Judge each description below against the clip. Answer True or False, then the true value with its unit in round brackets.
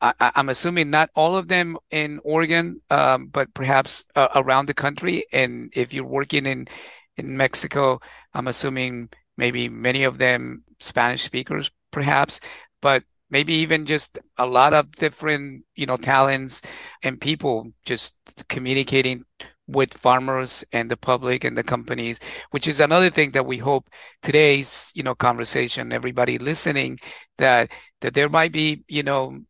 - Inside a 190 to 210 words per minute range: False (155 wpm)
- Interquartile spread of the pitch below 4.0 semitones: True (3.3 semitones)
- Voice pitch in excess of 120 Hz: True (135 Hz)